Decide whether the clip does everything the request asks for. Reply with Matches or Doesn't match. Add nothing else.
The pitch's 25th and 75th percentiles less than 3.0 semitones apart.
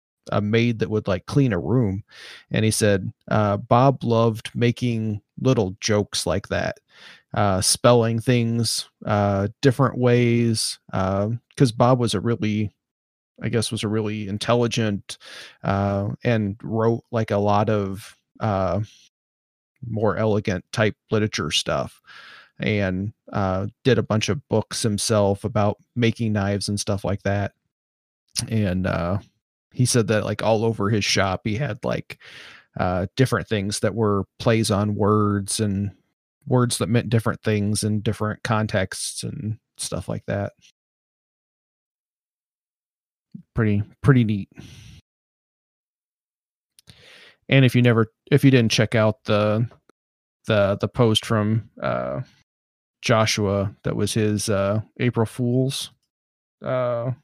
Matches